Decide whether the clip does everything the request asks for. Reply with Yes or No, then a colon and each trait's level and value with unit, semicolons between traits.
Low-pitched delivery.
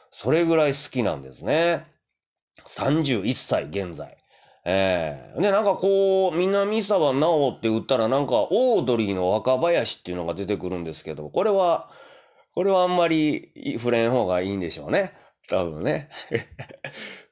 Yes: low, 130 Hz